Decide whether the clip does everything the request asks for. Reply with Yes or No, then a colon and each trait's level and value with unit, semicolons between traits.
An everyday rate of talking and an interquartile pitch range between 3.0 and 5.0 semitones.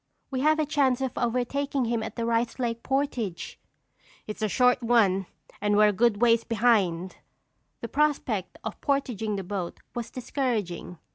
Yes: average, 160 wpm; average, 3.6 semitones